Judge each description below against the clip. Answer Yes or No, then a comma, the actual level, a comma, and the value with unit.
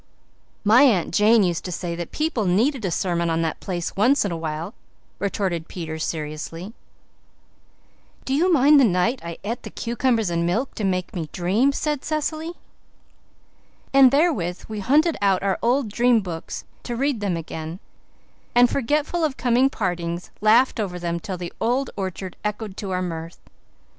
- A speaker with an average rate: Yes, average, 170 wpm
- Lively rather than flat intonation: Yes, wide, 6.8 semitones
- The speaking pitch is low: No, high, 205 Hz